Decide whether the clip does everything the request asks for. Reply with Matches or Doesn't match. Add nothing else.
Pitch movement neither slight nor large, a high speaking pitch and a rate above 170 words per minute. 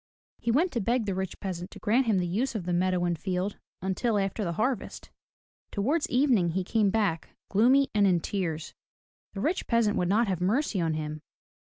Matches